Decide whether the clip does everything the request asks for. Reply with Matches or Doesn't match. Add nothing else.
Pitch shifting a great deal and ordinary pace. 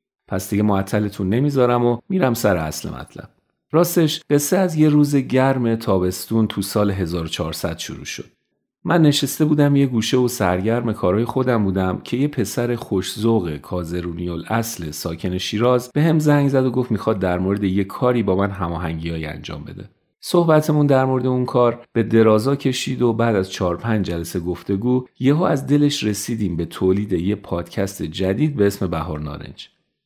Doesn't match